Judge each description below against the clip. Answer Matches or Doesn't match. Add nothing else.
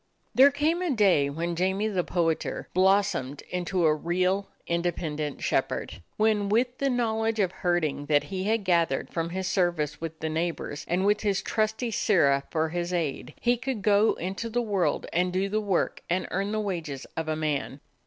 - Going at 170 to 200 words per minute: Matches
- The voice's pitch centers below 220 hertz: Matches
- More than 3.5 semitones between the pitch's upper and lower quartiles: Matches